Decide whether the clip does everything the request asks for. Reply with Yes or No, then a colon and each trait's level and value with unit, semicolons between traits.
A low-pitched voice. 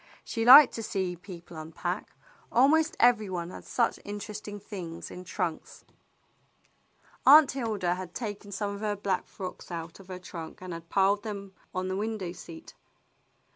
No: high, 195 Hz